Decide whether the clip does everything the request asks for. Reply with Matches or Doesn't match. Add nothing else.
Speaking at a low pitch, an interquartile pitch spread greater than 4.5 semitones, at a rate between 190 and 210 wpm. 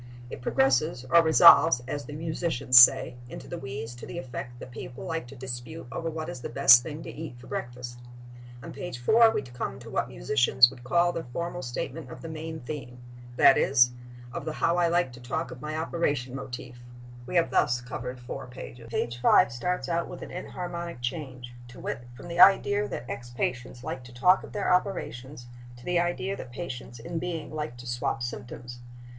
Matches